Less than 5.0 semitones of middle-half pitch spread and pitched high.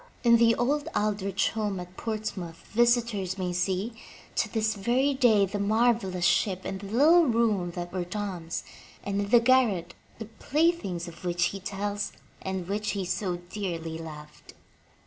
Yes: average, 4.0 semitones; high, 200 Hz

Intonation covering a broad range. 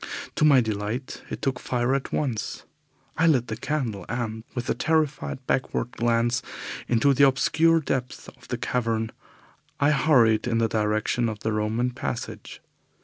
No: average, 3.4 semitones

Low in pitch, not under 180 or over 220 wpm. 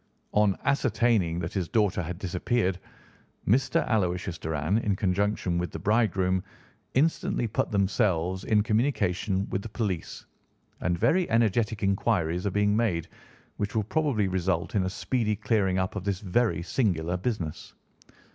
No: low, 100 Hz; average, 145 wpm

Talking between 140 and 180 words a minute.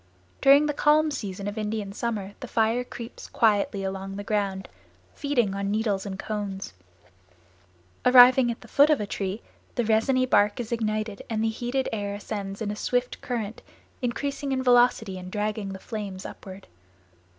Yes: average, 170 wpm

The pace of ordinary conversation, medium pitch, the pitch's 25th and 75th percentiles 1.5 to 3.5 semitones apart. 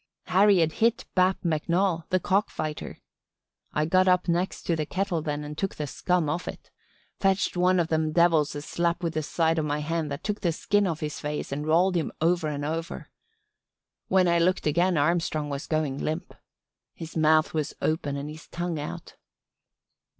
Yes: average, 190 wpm; medium, 165 Hz; average, 2.8 semitones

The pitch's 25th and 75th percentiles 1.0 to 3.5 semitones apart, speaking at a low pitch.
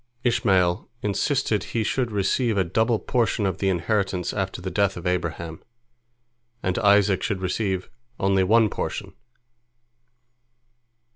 Yes: average, 3.0 semitones; low, 100 Hz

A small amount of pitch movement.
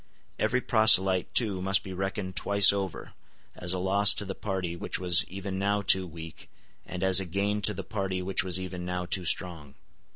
Yes: narrow, 1.7 semitones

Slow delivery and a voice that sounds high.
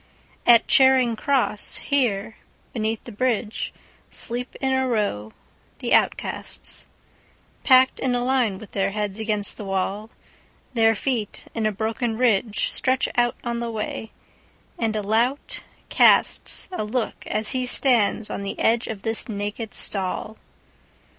Yes: slow, 125 wpm; high, 225 Hz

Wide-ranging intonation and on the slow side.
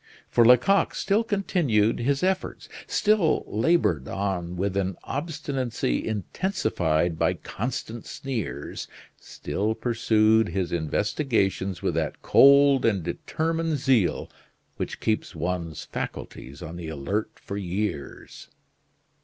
Yes: wide, 7.8 semitones; slow, 110 wpm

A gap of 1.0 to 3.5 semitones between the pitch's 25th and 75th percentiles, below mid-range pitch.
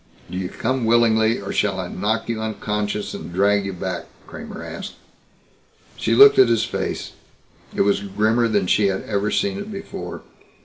Yes: narrow, 2.6 semitones; low, 105 Hz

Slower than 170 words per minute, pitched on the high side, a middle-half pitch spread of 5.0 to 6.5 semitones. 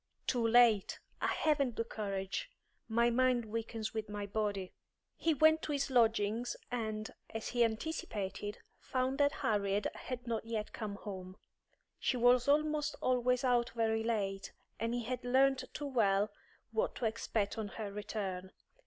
No: average, 155 wpm; high, 230 Hz; average, 3.3 semitones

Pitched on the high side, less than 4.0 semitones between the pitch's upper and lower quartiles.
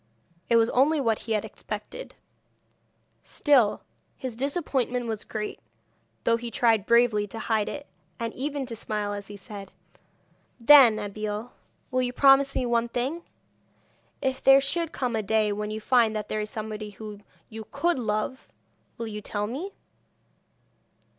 Yes: high, 230 Hz; average, 3.6 semitones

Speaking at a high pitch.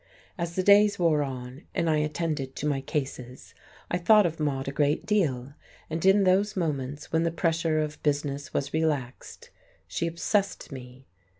No: medium, 155 Hz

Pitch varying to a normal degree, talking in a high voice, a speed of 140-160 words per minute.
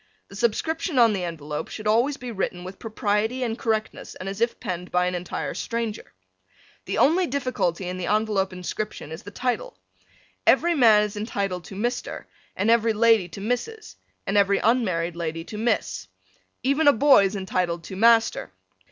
No: average, 4.5 semitones; high, 210 Hz; average, 175 wpm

